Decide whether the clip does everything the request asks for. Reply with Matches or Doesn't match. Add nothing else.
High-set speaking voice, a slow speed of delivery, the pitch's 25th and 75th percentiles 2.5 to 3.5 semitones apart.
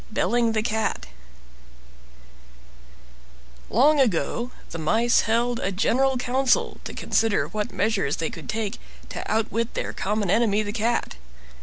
Matches